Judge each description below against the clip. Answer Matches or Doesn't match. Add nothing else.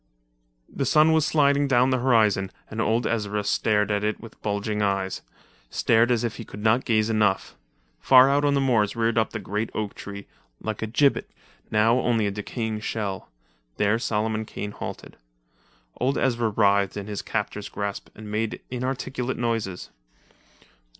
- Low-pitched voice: Matches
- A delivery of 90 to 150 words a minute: Doesn't match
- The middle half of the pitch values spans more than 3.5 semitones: Doesn't match